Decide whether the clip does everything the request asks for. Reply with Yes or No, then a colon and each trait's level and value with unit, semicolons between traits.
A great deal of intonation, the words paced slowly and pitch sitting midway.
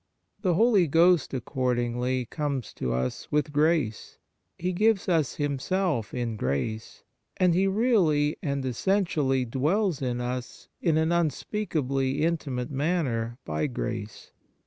Yes: wide, 5.7 semitones; slow, 125 wpm; medium, 145 Hz